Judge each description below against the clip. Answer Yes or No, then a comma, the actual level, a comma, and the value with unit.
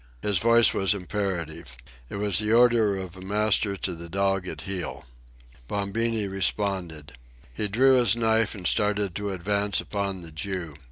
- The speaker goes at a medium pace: Yes, average, 160 wpm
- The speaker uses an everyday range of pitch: No, narrow, 2.3 semitones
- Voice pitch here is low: Yes, low, 100 Hz